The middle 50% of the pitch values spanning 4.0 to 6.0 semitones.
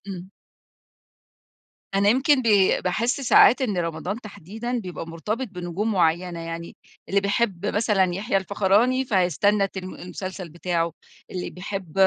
No: average, 3.3 semitones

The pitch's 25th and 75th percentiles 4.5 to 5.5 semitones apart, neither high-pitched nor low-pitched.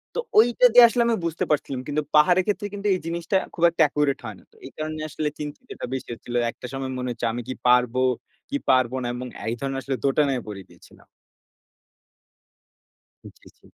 Yes: average, 5.1 semitones; medium, 145 Hz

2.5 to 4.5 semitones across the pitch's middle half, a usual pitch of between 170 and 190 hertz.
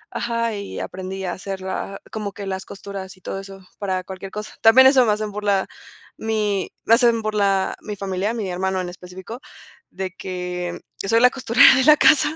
No: average, 2.9 semitones; high, 200 Hz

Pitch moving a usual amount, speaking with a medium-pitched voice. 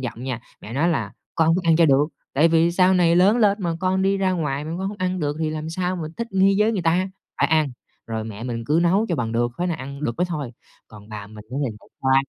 No: wide, 5.7 semitones; medium, 160 Hz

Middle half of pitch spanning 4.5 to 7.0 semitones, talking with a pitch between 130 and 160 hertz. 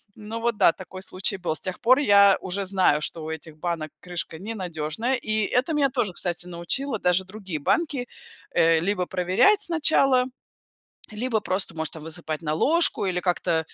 No: average, 5.2 semitones; high, 190 Hz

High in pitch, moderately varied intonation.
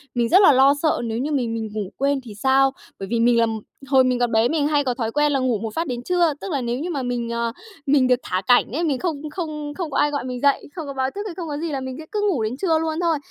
Yes: very high, 270 Hz; average, 4.2 semitones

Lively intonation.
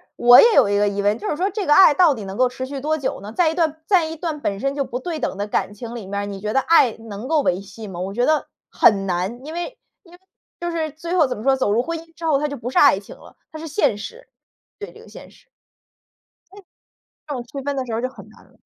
Yes: wide, 7.2 semitones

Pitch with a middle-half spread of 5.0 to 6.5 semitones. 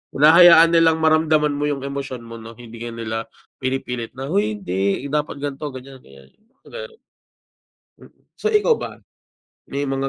Yes: average, 5.3 semitones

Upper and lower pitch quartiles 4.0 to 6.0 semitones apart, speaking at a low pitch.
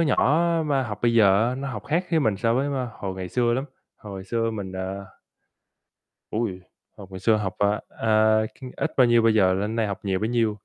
No: average, 3.4 semitones; low, 110 Hz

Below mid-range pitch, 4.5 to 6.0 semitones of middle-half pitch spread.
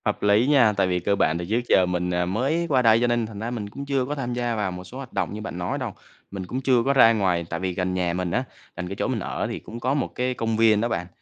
Yes: low, 110 Hz; average, 5.1 semitones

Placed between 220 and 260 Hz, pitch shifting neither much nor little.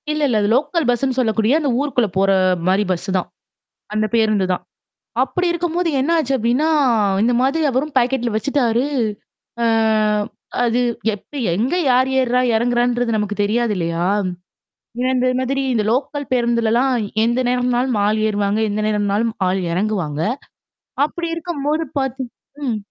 Yes: high, 240 Hz; average, 4.0 semitones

